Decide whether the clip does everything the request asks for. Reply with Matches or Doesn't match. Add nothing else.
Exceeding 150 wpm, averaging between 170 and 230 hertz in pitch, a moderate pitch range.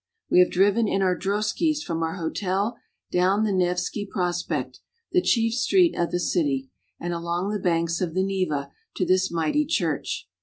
Matches